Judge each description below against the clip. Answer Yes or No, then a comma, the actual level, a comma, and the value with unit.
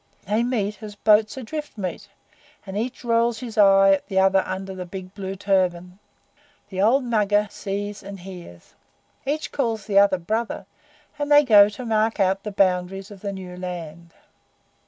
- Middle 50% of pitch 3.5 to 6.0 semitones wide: No, narrow, 2.6 semitones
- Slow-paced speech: No, average, 170 wpm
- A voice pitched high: Yes, high, 200 Hz